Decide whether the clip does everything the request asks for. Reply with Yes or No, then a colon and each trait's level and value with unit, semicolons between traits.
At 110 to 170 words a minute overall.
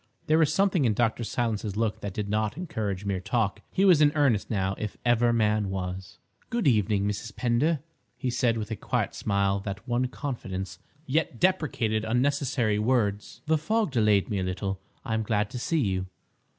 No: average, 185 wpm